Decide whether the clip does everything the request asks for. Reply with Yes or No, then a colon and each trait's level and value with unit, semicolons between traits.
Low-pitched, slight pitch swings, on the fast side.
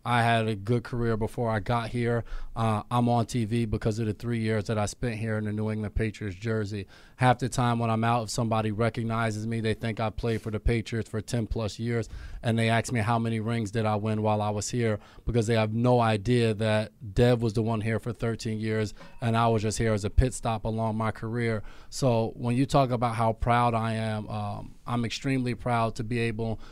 Yes: low, 115 Hz; narrow, 1.4 semitones; fast, 235 wpm